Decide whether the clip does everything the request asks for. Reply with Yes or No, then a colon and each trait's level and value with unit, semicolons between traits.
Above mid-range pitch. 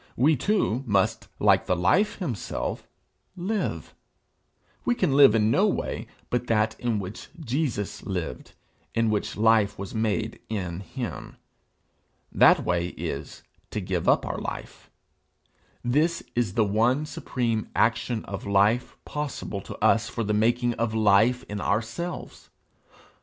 No: low, 110 Hz